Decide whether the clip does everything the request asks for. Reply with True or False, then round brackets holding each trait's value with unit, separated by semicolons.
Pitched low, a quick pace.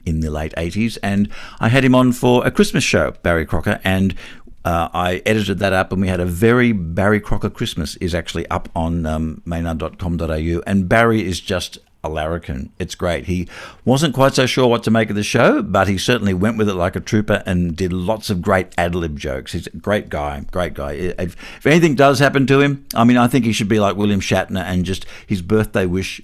True (95 Hz; 220 wpm)